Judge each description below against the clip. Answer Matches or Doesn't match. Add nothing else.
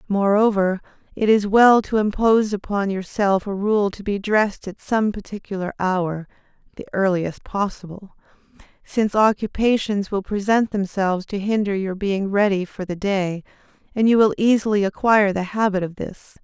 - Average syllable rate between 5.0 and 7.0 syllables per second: Doesn't match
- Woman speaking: Matches